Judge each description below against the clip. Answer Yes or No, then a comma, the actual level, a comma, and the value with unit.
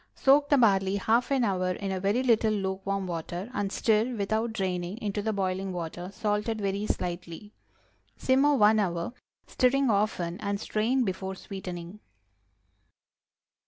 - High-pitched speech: Yes, high, 200 Hz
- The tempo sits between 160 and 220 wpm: No, average, 140 wpm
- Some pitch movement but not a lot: Yes, average, 3.0 semitones